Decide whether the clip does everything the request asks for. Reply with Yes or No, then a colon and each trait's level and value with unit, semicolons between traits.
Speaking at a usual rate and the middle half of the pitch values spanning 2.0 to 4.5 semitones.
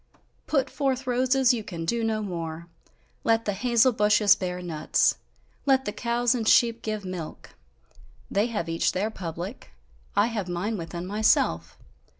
No: average, 150 wpm; average, 5.0 semitones